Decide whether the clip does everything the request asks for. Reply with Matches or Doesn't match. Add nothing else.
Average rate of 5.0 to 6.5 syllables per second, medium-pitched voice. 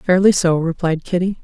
Matches